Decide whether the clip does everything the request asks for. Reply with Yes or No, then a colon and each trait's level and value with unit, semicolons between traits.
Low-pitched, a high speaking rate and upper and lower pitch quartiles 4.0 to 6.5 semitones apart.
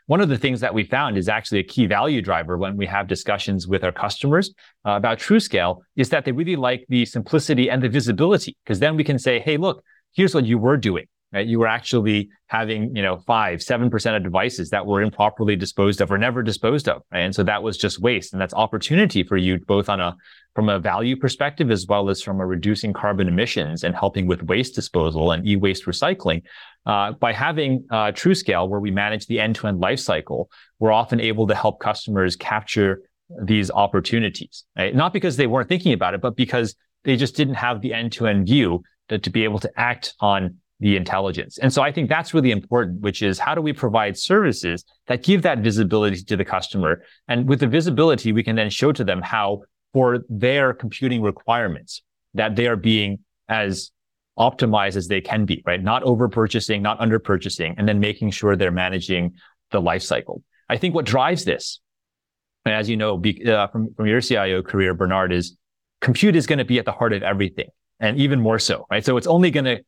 Yes: low, 110 Hz; fast, 210 wpm; average, 4.3 semitones